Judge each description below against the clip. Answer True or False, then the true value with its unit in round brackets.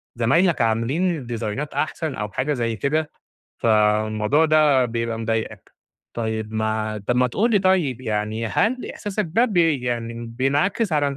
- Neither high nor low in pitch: False (125 Hz)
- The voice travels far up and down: True (6.0 semitones)